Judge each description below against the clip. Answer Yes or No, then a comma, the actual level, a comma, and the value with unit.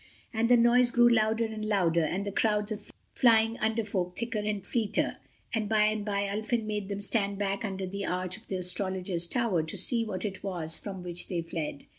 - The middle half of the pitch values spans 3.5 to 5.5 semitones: No, average, 3.1 semitones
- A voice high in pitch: Yes, high, 205 Hz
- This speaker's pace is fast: Yes, fast, 210 wpm